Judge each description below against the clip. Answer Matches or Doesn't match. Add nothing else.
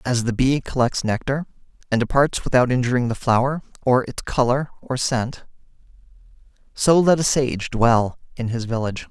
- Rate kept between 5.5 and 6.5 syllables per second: Doesn't match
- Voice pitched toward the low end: Matches